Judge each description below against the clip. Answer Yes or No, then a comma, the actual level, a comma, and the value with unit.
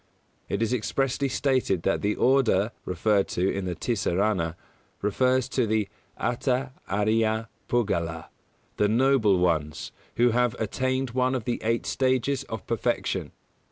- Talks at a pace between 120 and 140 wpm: Yes, slow, 135 wpm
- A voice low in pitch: Yes, low, 110 Hz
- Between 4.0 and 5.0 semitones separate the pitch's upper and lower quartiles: Yes, average, 4.5 semitones